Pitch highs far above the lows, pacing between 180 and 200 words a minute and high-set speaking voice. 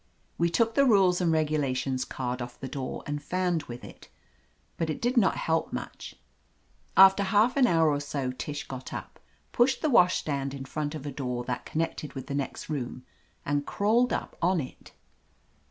No: wide, 5.8 semitones; average, 185 wpm; medium, 155 Hz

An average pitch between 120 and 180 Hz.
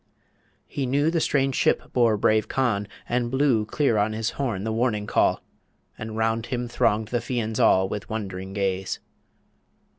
No: low, 110 Hz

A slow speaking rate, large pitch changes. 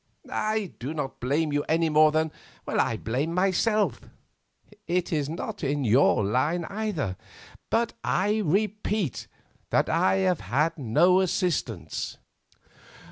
Yes: slow, 115 wpm; wide, 6.2 semitones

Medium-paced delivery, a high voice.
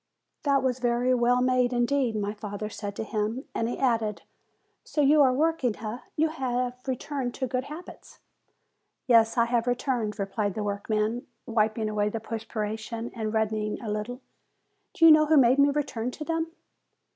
Yes: average, 175 wpm; high, 240 Hz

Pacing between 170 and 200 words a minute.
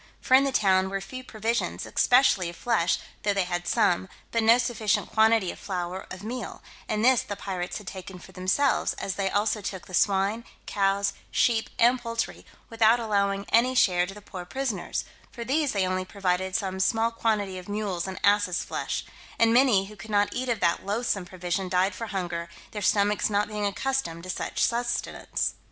Yes: average, 190 wpm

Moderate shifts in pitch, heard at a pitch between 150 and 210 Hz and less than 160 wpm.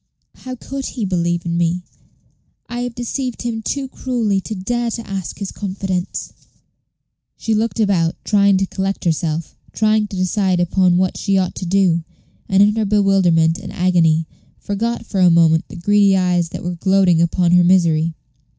No: average, 3.4 semitones; high, 190 Hz; average, 170 wpm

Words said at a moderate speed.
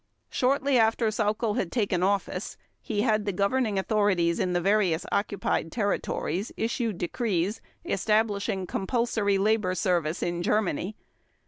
No: slow, 125 wpm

